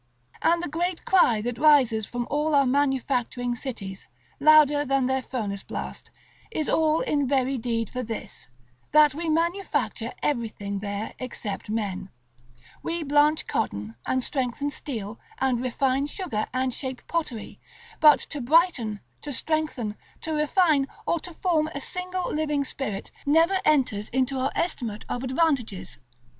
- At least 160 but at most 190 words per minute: No, average, 145 wpm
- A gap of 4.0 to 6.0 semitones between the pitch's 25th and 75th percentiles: Yes, average, 4.6 semitones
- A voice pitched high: Yes, very high, 270 Hz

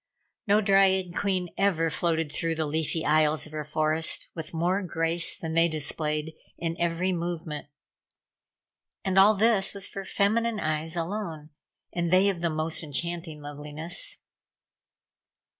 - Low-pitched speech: No, medium, 165 Hz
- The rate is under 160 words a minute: Yes, average, 140 wpm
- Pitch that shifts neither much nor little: Yes, average, 3.2 semitones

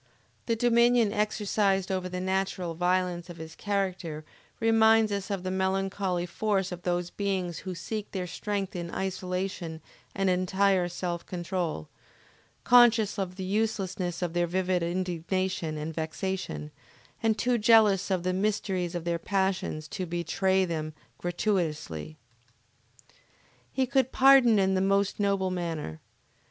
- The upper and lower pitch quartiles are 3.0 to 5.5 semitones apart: No, narrow, 2.5 semitones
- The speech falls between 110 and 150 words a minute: Yes, slow, 135 wpm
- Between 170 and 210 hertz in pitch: Yes, medium, 185 Hz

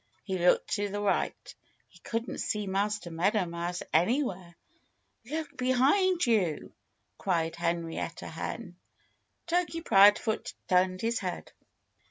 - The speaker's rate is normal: No, slow, 115 wpm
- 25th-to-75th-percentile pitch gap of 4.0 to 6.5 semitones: Yes, average, 5.0 semitones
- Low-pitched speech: No, high, 200 Hz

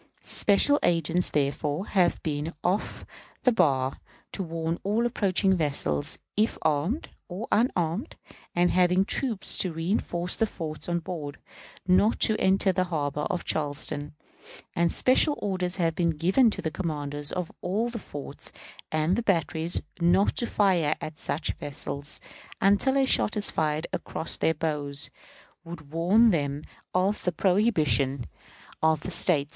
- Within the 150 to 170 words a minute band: No, average, 140 wpm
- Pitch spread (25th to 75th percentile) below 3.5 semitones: No, average, 4.4 semitones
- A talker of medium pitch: Yes, medium, 170 Hz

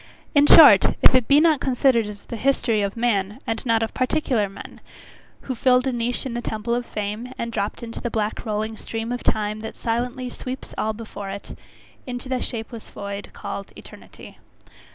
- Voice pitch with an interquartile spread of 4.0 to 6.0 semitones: No, average, 2.8 semitones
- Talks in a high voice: Yes, high, 230 Hz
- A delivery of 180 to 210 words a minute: Yes, average, 190 wpm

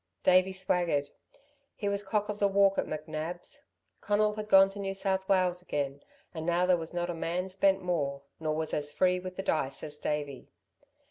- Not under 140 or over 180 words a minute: No, average, 195 wpm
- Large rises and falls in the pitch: No, average, 3.9 semitones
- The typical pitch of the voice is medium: Yes, medium, 180 Hz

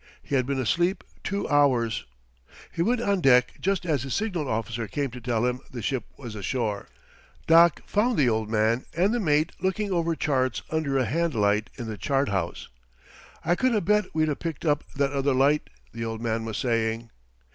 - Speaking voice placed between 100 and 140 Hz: Yes, low, 135 Hz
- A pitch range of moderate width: No, wide, 6.5 semitones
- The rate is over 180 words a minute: Yes, average, 200 wpm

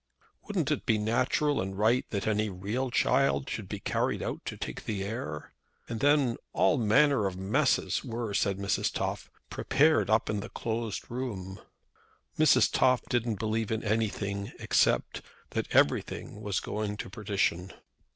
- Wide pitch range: No, average, 3.4 semitones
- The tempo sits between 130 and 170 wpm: Yes, average, 155 wpm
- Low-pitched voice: Yes, low, 110 Hz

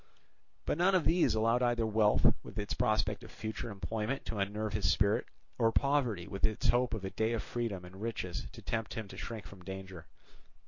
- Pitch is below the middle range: Yes, low, 110 Hz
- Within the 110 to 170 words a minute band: No, average, 200 wpm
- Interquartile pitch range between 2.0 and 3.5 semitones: Yes, average, 2.8 semitones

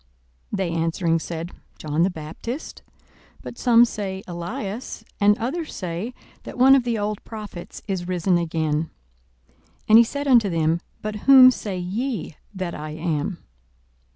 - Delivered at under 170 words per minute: Yes, average, 150 wpm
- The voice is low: No, high, 190 Hz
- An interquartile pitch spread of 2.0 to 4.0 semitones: No, wide, 5.5 semitones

